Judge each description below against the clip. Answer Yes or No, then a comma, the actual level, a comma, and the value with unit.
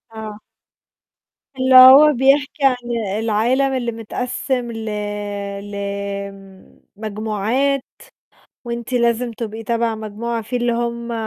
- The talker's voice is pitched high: Yes, high, 235 Hz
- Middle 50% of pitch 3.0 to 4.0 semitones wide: No, narrow, 2.4 semitones